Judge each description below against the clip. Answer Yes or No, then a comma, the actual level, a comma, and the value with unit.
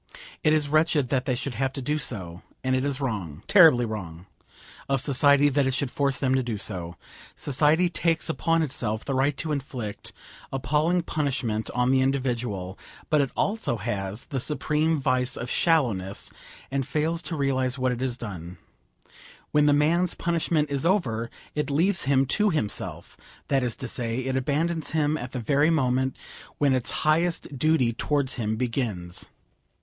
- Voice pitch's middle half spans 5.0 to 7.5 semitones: No, average, 3.9 semitones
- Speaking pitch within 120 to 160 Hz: Yes, low, 135 Hz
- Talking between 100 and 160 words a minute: No, average, 170 wpm